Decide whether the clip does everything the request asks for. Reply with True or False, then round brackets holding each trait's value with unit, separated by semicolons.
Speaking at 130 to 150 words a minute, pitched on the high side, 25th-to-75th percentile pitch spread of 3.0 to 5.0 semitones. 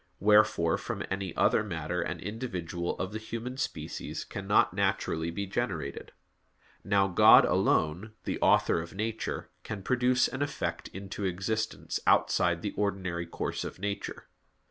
False (140 wpm; 95 Hz; 4.1 semitones)